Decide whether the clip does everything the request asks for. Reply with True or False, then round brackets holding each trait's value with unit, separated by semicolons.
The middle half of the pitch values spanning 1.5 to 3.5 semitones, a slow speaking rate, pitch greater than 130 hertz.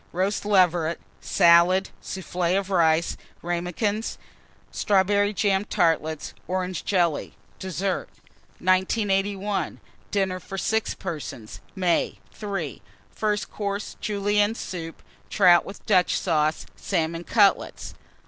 True (2.9 semitones; 100 wpm; 185 Hz)